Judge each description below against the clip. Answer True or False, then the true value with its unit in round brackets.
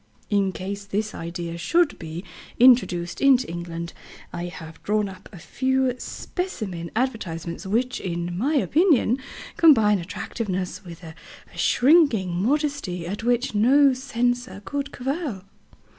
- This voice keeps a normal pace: False (125 wpm)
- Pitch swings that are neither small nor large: False (6.7 semitones)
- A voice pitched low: False (210 Hz)